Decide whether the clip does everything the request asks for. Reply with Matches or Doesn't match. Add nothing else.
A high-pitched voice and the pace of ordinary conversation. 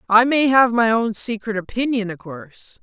Matches